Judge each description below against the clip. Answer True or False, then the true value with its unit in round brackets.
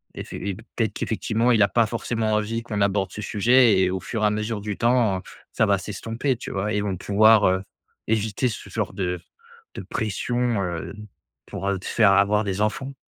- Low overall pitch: True (105 Hz)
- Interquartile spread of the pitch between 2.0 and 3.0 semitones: True (2.5 semitones)